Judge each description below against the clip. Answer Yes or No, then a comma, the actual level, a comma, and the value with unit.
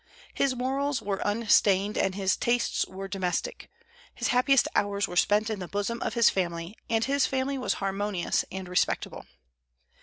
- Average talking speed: Yes, average, 160 wpm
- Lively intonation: No, average, 4.3 semitones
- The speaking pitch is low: No, high, 205 Hz